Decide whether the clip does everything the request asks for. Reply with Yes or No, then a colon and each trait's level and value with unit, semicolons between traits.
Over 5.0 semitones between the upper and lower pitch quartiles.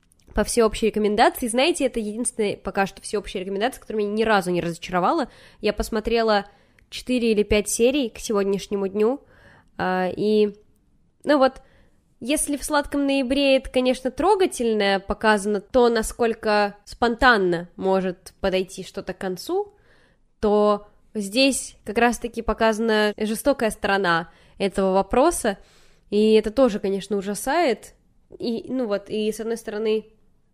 No: average, 3.4 semitones